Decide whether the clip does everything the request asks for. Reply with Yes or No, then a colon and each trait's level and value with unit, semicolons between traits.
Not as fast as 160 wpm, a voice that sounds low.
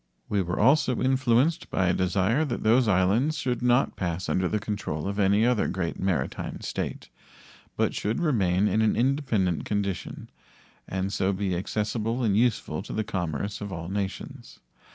No: average, 165 wpm; low, 105 Hz